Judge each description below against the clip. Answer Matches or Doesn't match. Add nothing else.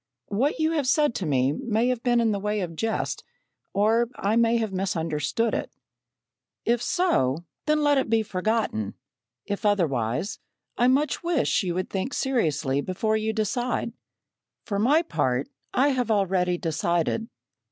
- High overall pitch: Matches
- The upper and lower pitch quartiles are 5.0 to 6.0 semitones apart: Matches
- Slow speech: Doesn't match